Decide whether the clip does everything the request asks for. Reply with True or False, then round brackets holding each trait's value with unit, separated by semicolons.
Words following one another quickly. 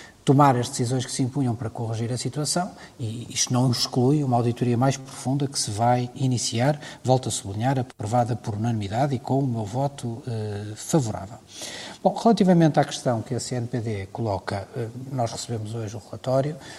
False (175 wpm)